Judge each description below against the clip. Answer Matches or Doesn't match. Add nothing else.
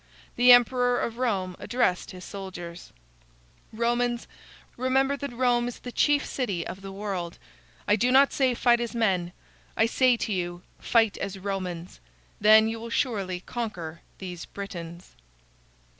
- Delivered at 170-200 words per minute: Doesn't match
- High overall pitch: Matches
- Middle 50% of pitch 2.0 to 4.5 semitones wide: Doesn't match